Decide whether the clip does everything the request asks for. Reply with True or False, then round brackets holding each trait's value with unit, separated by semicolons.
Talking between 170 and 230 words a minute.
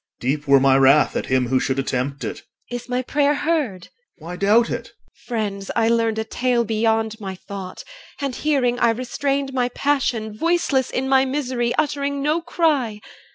True (190 wpm)